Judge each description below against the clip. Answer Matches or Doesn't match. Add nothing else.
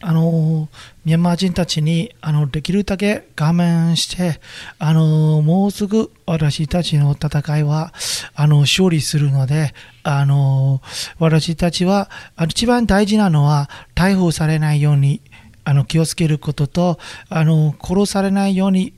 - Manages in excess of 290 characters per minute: Doesn't match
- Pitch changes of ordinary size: Matches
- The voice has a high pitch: Doesn't match